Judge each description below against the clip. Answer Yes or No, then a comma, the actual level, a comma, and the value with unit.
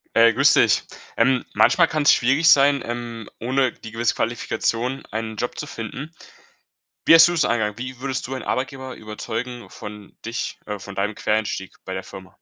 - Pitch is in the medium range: No, low, 120 Hz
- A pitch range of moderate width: Yes, average, 3.4 semitones